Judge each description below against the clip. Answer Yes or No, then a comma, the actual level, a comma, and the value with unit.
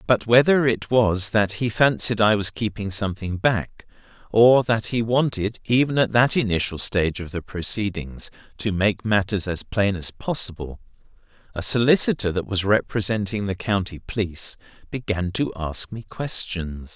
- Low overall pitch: Yes, low, 105 Hz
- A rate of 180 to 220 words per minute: No, average, 155 wpm